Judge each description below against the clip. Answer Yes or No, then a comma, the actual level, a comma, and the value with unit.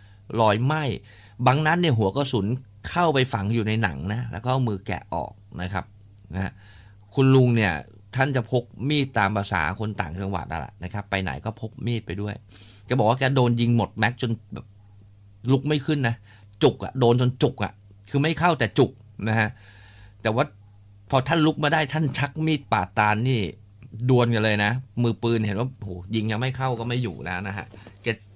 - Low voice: Yes, low, 110 Hz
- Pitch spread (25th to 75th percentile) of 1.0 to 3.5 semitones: No, average, 3.9 semitones